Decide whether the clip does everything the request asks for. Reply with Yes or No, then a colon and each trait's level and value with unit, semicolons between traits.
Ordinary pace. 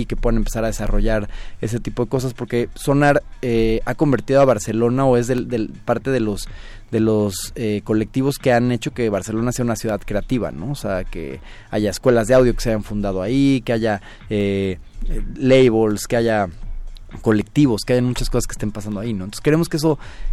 No: fast, 205 wpm